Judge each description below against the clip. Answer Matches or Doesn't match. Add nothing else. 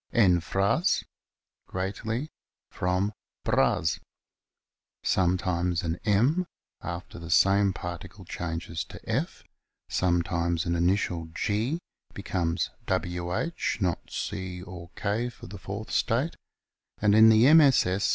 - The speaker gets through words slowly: Matches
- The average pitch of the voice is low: Matches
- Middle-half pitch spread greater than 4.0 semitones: Doesn't match